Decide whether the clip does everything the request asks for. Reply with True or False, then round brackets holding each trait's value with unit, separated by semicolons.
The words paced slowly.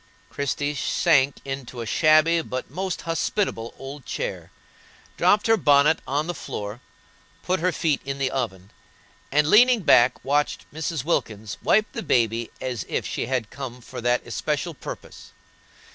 False (150 wpm)